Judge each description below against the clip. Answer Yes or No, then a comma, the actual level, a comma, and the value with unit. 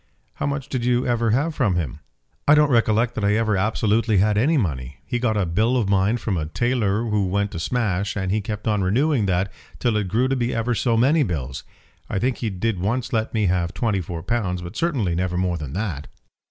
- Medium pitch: No, low, 105 Hz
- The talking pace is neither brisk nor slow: No, fast, 230 wpm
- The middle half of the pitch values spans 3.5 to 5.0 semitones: Yes, average, 4.5 semitones